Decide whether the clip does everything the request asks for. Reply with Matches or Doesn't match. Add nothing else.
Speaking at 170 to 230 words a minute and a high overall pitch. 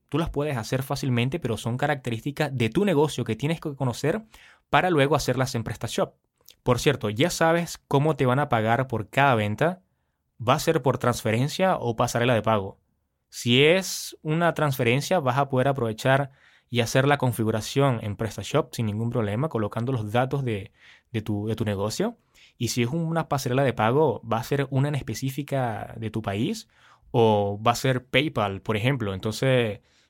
Doesn't match